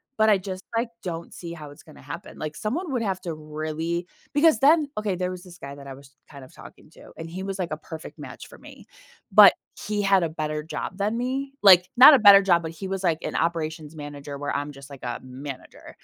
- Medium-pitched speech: Yes, medium, 170 Hz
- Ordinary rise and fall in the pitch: Yes, average, 4.7 semitones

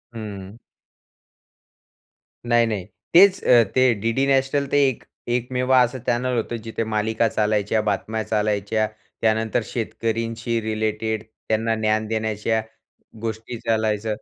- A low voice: Yes, low, 110 Hz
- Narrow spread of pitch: Yes, narrow, 1.6 semitones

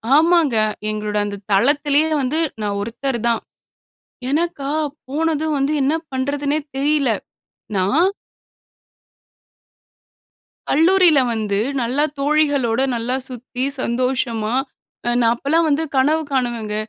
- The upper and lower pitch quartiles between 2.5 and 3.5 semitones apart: No, average, 4.3 semitones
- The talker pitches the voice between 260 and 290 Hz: Yes, very high, 270 Hz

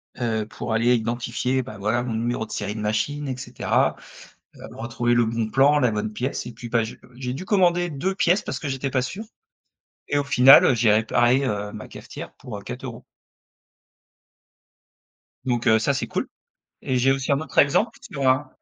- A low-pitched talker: Yes, low, 125 Hz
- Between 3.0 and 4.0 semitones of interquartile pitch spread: Yes, average, 3.3 semitones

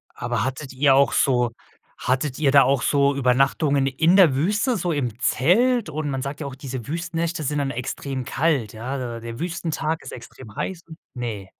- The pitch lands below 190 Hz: Yes, medium, 140 Hz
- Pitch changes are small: No, average, 3.9 semitones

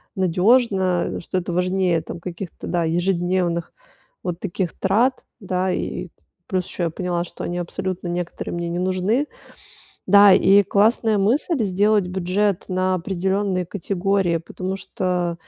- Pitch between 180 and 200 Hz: Yes, medium, 185 Hz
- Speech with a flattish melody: Yes, narrow, 2.0 semitones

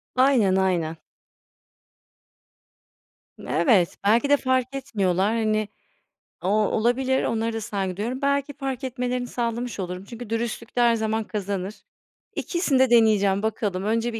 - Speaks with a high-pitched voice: Yes, high, 225 Hz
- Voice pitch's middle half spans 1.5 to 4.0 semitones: Yes, average, 3.7 semitones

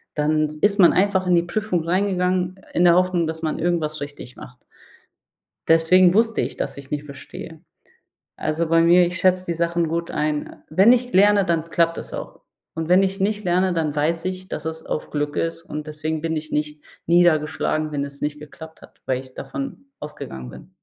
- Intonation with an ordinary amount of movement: Yes, average, 3.2 semitones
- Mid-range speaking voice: Yes, medium, 165 Hz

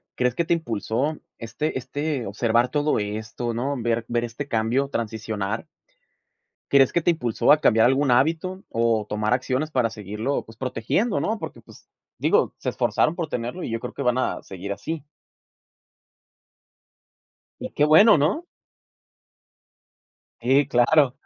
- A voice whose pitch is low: Yes, low, 125 Hz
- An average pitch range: Yes, average, 4.7 semitones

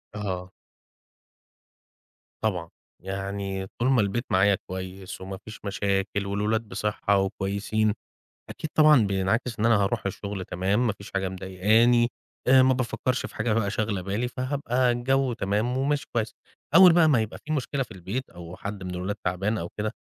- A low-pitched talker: Yes, low, 105 Hz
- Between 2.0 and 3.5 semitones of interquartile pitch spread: No, average, 3.9 semitones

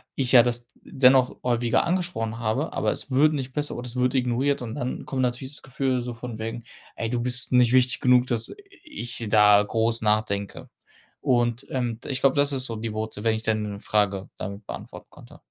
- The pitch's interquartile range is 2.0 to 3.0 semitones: Yes, narrow, 2.6 semitones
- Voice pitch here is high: No, low, 120 Hz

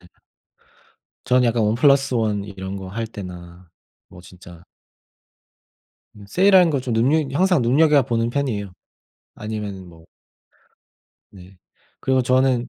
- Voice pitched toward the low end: Yes, low, 115 Hz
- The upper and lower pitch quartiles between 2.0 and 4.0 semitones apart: No, wide, 5.5 semitones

